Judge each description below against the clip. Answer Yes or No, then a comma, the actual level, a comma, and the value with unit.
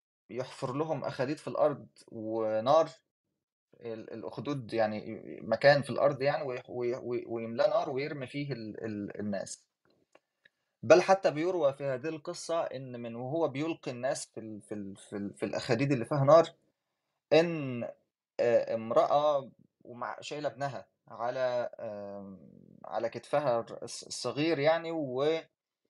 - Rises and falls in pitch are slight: No, wide, 5.6 semitones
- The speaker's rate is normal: Yes, average, 115 wpm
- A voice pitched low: Yes, low, 130 Hz